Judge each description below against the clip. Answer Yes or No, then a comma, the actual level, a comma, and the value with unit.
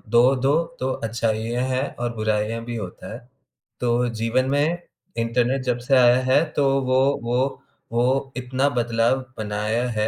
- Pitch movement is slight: Yes, narrow, 2.2 semitones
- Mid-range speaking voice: No, low, 120 Hz